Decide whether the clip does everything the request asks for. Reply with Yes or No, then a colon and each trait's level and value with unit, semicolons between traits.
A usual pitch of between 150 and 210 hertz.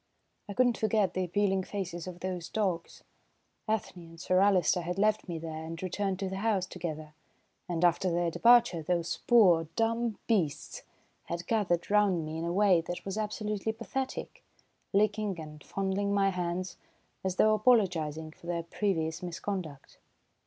Yes: medium, 185 Hz